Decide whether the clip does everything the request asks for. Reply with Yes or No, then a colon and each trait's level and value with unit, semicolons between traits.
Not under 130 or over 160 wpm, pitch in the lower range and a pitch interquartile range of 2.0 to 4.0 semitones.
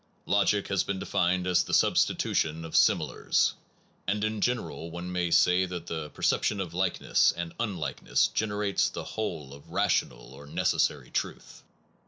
Yes: average, 155 wpm; very low, 90 Hz; average, 3.6 semitones